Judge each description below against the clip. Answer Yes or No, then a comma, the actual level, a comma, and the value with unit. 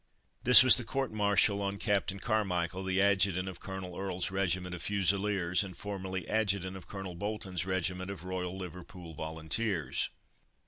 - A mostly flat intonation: Yes, narrow, 1.9 semitones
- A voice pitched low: Yes, very low, 95 Hz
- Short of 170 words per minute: Yes, average, 150 wpm